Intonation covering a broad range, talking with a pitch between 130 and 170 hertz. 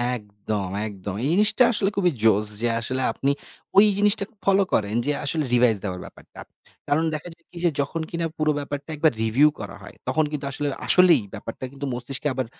Yes: wide, 6.6 semitones; medium, 140 Hz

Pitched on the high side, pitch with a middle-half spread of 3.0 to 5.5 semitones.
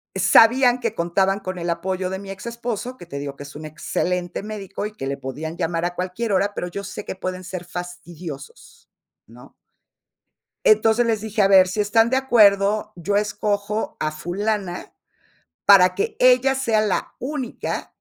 Yes: high, 195 Hz; average, 3.8 semitones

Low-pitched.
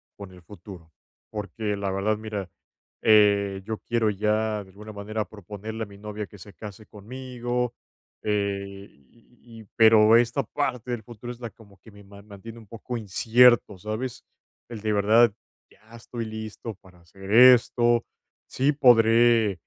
Yes: low, 110 Hz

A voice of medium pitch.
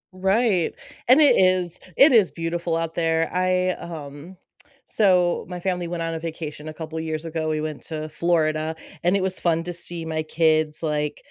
Yes: medium, 165 Hz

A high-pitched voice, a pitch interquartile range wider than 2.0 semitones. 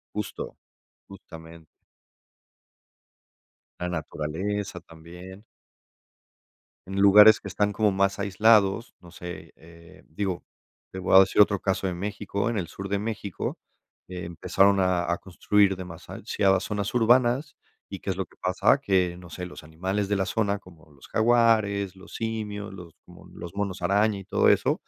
No: very low, 95 Hz; narrow, 2.6 semitones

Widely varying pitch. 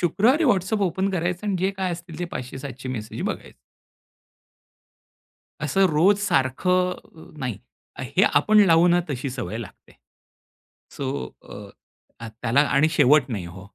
Yes: wide, 6.4 semitones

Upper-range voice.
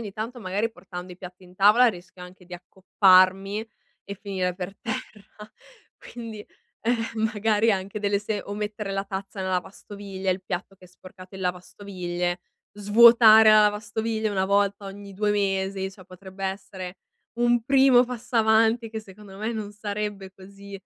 Yes: high, 200 Hz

